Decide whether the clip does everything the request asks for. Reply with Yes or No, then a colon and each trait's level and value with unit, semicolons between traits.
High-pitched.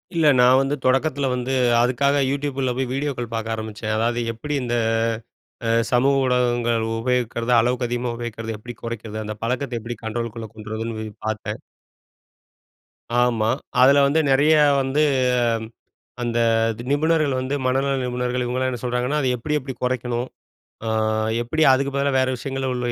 No: low, 125 Hz